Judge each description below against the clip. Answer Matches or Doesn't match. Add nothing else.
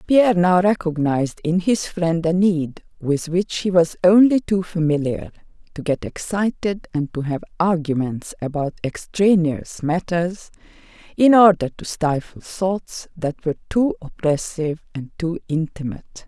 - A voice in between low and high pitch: Matches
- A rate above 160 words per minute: Doesn't match